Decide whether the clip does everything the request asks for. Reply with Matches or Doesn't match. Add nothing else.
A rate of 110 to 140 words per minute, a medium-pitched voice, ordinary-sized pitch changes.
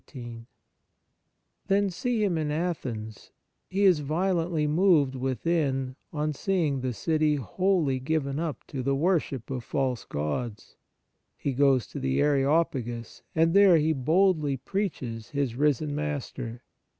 Matches